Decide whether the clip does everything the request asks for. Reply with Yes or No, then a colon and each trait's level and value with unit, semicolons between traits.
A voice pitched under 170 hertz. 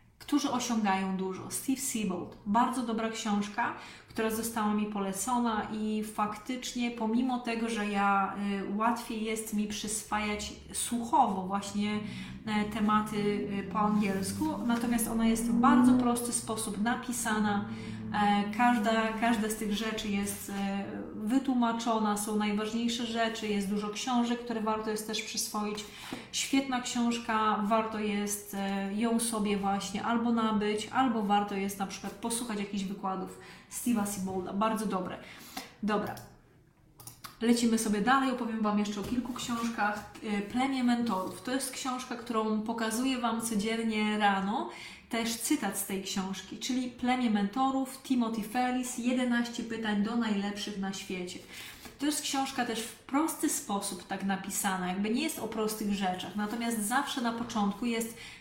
No: high, 220 Hz